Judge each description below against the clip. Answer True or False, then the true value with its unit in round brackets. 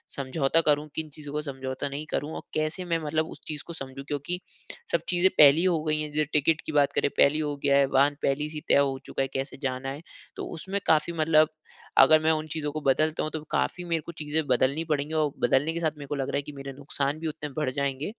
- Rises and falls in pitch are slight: True (2.2 semitones)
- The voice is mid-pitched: True (150 Hz)